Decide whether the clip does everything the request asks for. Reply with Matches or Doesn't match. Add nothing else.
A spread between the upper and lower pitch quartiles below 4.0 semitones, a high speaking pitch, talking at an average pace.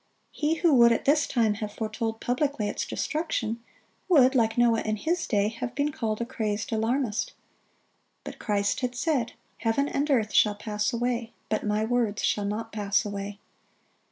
Matches